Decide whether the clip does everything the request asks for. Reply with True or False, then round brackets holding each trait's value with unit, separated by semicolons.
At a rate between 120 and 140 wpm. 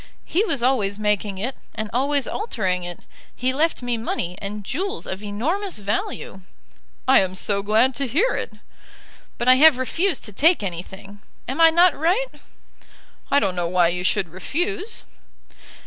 False (165 wpm)